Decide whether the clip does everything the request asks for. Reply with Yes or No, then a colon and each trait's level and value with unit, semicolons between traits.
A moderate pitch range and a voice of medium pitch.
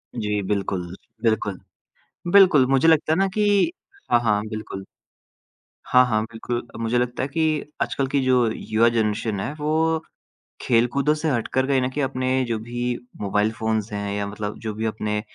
No: average, 4.0 semitones; low, 120 Hz